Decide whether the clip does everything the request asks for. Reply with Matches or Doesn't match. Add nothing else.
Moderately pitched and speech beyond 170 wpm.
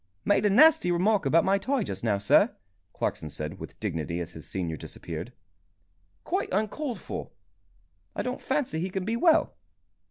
Doesn't match